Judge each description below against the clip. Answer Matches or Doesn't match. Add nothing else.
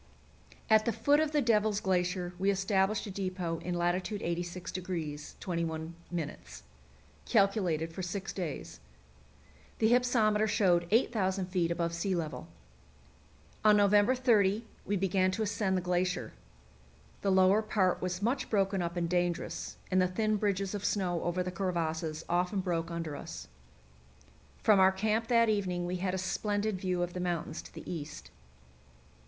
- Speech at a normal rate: Matches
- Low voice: Doesn't match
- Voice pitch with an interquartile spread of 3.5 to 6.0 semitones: Doesn't match